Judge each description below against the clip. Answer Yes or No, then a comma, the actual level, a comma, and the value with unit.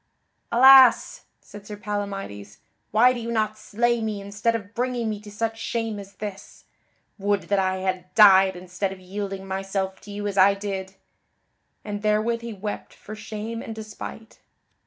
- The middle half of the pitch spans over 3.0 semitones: No, narrow, 2.4 semitones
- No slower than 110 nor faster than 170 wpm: Yes, average, 165 wpm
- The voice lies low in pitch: No, high, 205 Hz